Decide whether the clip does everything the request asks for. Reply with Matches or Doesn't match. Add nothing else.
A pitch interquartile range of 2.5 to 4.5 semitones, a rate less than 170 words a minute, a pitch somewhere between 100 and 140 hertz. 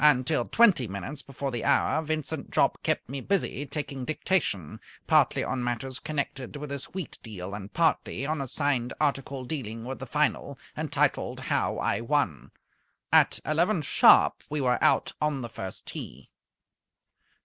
Matches